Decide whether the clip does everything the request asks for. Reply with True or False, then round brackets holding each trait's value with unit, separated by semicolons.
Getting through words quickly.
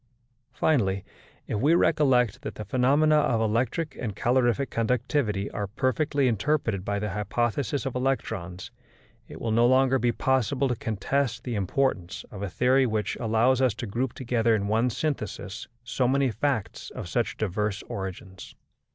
False (155 wpm)